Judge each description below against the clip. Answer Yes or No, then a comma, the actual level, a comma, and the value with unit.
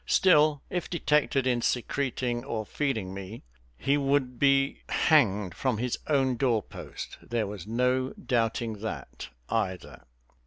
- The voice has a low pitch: Yes, low, 125 Hz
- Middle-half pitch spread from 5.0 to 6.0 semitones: No, average, 3.9 semitones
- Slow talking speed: Yes, slow, 130 wpm